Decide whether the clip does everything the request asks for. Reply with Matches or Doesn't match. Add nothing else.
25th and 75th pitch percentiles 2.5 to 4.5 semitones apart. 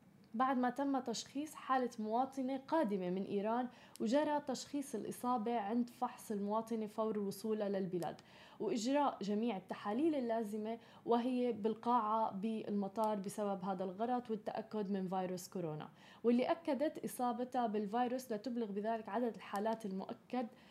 Matches